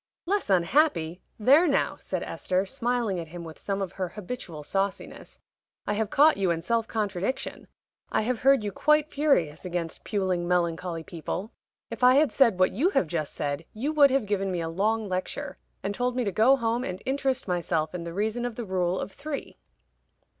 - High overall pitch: Yes, high, 200 Hz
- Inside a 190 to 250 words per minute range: Yes, average, 195 wpm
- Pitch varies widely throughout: Yes, wide, 6.2 semitones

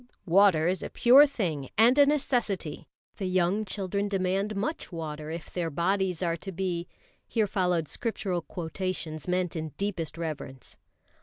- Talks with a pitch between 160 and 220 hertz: Yes, medium, 185 Hz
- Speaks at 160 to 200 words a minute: No, average, 150 wpm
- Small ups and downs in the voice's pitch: No, average, 3.4 semitones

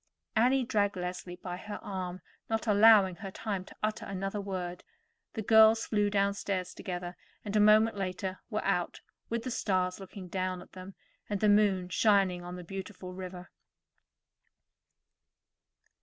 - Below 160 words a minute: Yes, average, 150 wpm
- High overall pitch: Yes, high, 195 Hz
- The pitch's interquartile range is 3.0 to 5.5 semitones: No, narrow, 2.5 semitones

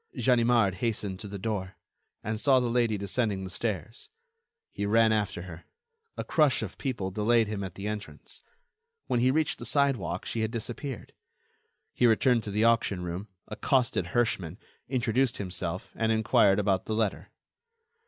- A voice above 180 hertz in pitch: No, low, 110 Hz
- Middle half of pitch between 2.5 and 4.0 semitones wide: Yes, average, 3.6 semitones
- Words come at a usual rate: Yes, average, 160 wpm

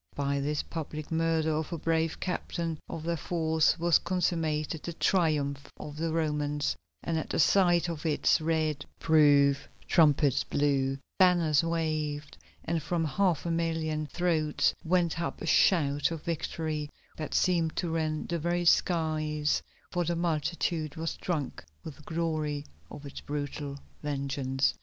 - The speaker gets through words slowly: No, average, 145 wpm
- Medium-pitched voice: Yes, medium, 155 Hz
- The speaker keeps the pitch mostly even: Yes, narrow, 2.1 semitones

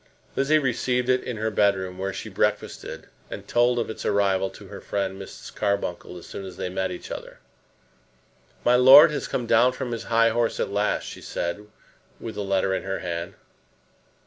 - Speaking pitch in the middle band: No, low, 105 Hz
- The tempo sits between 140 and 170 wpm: No, average, 190 wpm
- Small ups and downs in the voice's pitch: No, average, 4.1 semitones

